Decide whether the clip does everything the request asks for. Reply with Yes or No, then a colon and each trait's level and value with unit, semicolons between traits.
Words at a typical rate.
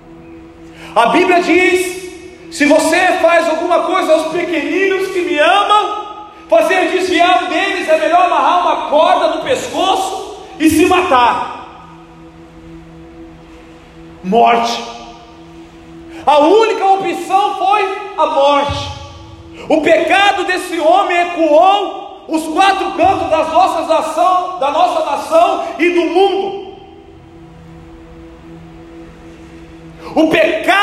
No: slow, 100 wpm